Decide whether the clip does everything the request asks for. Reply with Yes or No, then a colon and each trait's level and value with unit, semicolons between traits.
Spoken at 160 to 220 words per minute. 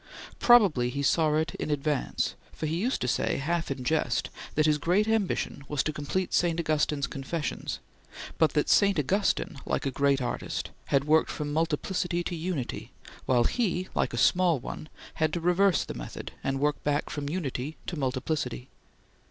Yes: average, 175 wpm